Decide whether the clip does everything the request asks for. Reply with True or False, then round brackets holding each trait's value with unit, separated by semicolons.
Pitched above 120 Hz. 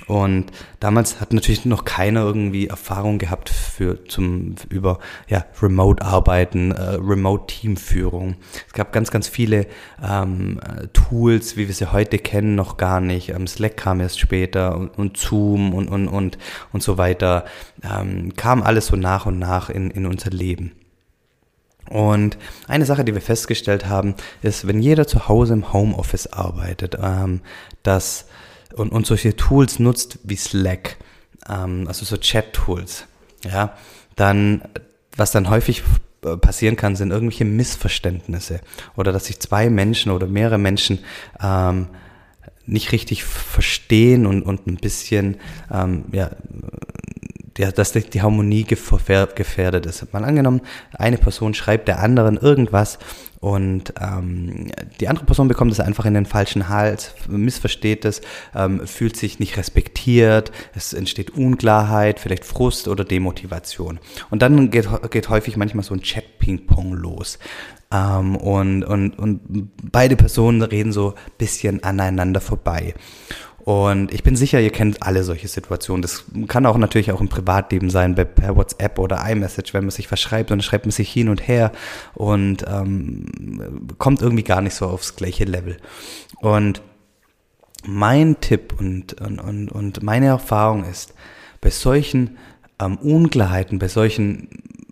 False (100 Hz)